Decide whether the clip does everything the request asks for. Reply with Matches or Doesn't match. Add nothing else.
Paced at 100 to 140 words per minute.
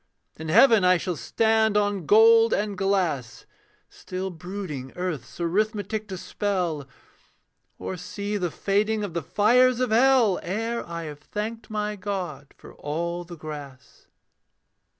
Matches